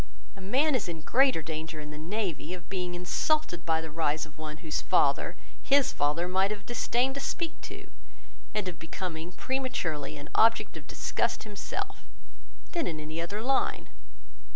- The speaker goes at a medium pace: Yes, average, 170 wpm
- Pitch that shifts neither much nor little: No, wide, 6.3 semitones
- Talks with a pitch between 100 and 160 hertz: No, medium, 175 Hz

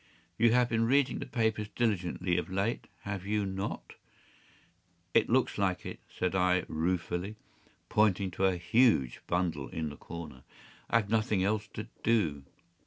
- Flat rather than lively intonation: No, average, 3.7 semitones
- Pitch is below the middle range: Yes, very low, 95 Hz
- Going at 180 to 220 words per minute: No, average, 160 wpm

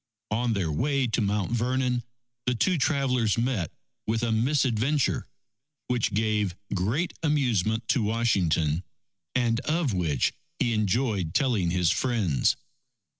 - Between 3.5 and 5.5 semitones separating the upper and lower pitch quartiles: Yes, average, 4.4 semitones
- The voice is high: No, low, 115 Hz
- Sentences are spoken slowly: Yes, slow, 125 wpm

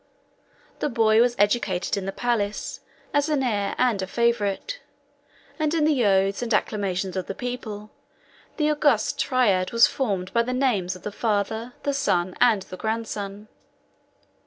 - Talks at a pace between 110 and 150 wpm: No, average, 160 wpm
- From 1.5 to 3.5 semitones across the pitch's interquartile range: No, average, 4.0 semitones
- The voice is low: No, high, 220 Hz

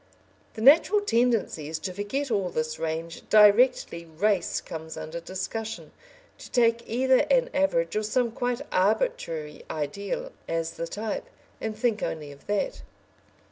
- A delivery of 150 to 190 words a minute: No, average, 140 wpm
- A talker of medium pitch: No, high, 210 Hz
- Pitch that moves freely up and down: Yes, wide, 6.7 semitones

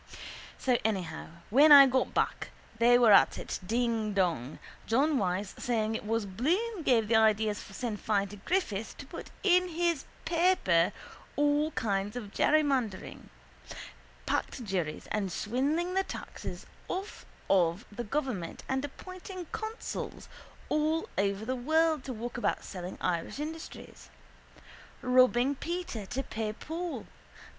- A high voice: Yes, high, 245 Hz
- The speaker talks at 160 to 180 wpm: No, slow, 135 wpm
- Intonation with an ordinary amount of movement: No, wide, 6.9 semitones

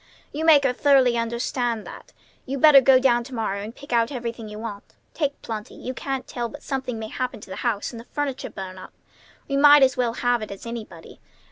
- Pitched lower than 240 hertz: No, high, 245 Hz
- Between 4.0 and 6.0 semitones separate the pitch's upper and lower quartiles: No, average, 3.2 semitones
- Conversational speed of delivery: No, fast, 225 wpm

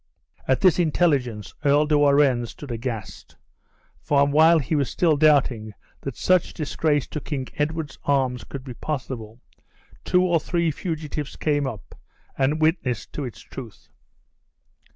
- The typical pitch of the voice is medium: Yes, medium, 145 Hz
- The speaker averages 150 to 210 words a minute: No, average, 140 wpm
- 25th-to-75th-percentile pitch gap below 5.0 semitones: Yes, average, 3.6 semitones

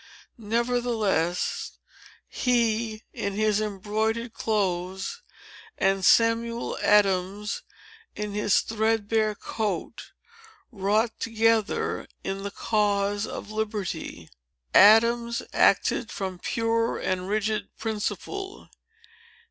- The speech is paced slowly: Yes, slow, 85 wpm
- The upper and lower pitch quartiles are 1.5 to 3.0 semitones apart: Yes, narrow, 2.4 semitones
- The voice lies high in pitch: Yes, high, 215 Hz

